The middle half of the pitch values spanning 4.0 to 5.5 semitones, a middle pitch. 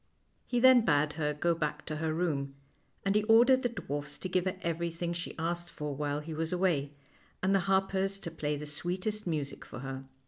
Yes: average, 4.3 semitones; medium, 170 Hz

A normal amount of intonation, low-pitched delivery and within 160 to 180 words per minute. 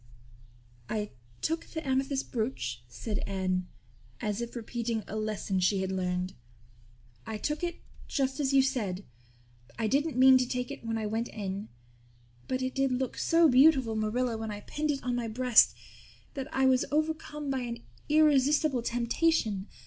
No: average, 4.1 semitones; high, 245 Hz; average, 165 wpm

